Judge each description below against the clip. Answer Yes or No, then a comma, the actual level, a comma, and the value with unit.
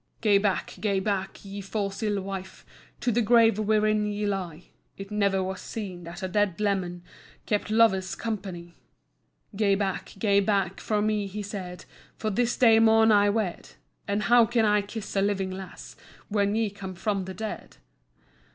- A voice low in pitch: No, high, 205 Hz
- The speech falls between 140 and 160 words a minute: No, average, 170 wpm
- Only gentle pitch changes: Yes, narrow, 1.9 semitones